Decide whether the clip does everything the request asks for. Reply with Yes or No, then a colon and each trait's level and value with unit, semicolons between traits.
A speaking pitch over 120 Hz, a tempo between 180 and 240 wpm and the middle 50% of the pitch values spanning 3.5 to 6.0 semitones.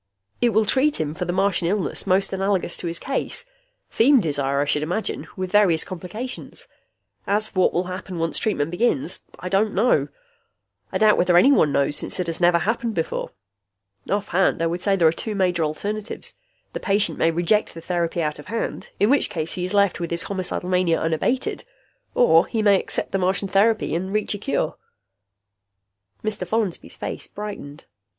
Yes: medium, 185 Hz; average, 185 wpm; average, 3.9 semitones